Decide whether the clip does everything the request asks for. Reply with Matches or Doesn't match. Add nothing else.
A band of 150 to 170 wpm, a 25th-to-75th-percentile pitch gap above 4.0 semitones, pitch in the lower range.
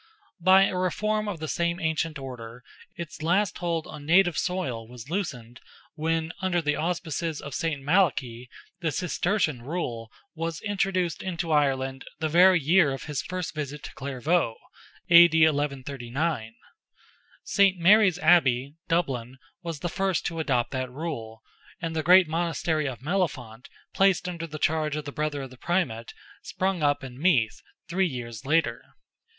Doesn't match